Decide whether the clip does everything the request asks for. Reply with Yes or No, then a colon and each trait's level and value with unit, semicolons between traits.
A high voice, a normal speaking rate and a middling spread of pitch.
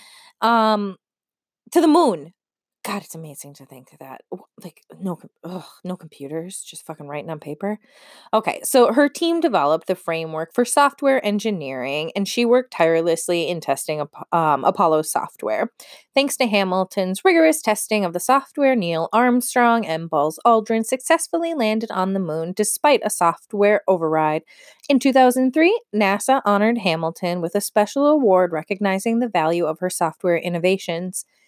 No: high, 200 Hz; average, 150 wpm; wide, 7.1 semitones